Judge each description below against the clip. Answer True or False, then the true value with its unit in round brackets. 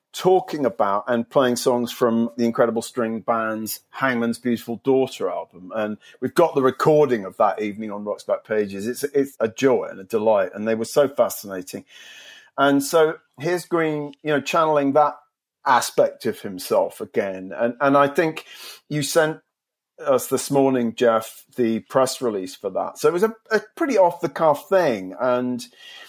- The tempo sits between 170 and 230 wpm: True (175 wpm)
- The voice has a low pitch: True (130 Hz)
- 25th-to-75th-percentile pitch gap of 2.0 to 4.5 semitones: False (4.9 semitones)